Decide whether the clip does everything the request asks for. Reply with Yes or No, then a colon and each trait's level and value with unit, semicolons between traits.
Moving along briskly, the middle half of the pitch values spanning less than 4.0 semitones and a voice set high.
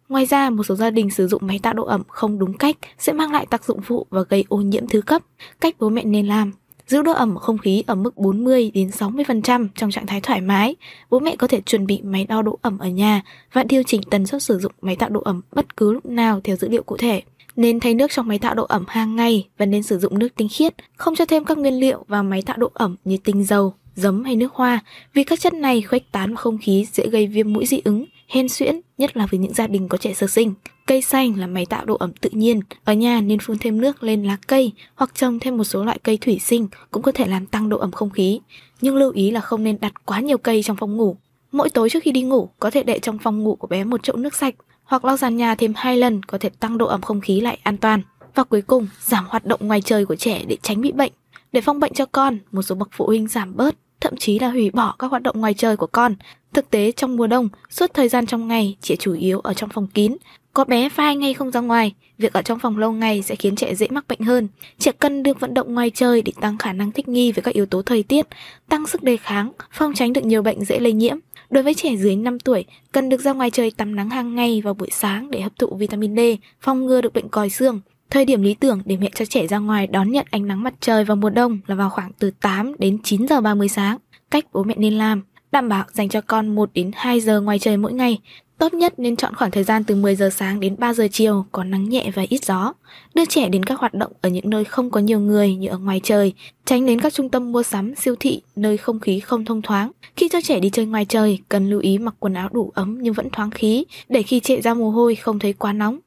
Yes: fast, 275 wpm; average, 3.6 semitones; high, 225 Hz